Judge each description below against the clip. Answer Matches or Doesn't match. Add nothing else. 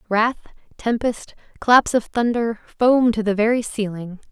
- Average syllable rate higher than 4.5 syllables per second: Doesn't match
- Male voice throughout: Doesn't match